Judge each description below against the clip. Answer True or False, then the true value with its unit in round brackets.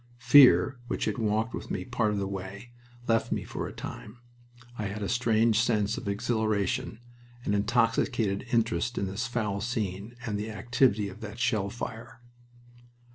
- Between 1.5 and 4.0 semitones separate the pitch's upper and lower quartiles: True (2.8 semitones)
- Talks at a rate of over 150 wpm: True (165 wpm)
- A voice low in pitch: True (110 Hz)